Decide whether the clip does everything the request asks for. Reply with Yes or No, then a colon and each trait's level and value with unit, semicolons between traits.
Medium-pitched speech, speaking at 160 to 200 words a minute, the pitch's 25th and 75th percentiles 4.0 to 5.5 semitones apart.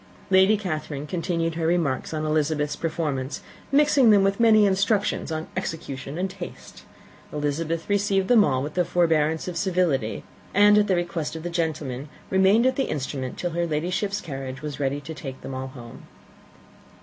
Yes: medium, 165 Hz; average, 170 wpm; average, 4.5 semitones